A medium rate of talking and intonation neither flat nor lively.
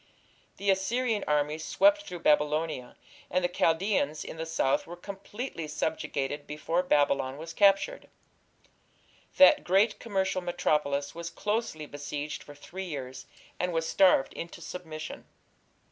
No: slow, 130 wpm; average, 4.4 semitones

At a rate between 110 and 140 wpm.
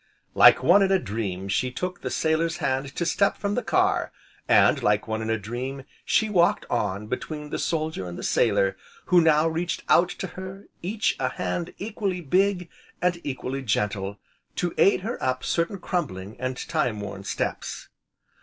No: average, 175 wpm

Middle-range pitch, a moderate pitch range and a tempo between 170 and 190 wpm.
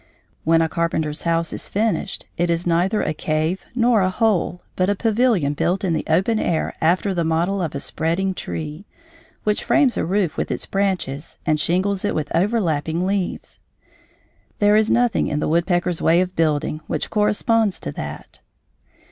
Yes: medium, 180 Hz; average, 3.9 semitones; average, 175 wpm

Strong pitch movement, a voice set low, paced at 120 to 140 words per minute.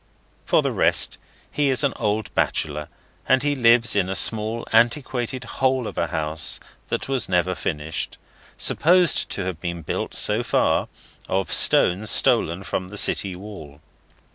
No: wide, 6.1 semitones; low, 105 Hz; average, 150 wpm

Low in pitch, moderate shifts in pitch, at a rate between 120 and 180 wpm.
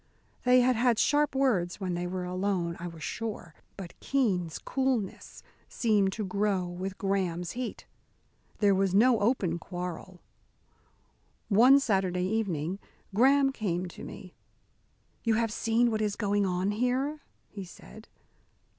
No: high, 200 Hz; average, 4.5 semitones; slow, 135 wpm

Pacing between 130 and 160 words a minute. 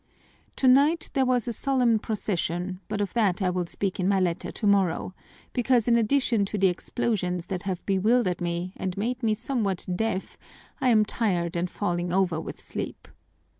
No: average, 170 wpm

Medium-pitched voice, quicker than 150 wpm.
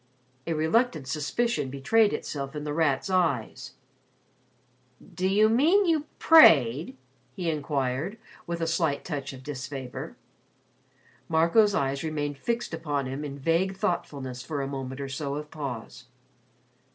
No: medium, 150 Hz; average, 140 wpm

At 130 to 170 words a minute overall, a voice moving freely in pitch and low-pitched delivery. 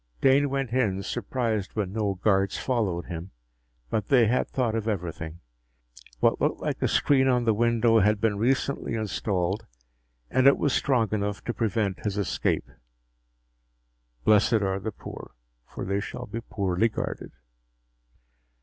No: average, 150 wpm; average, 3.4 semitones; low, 110 Hz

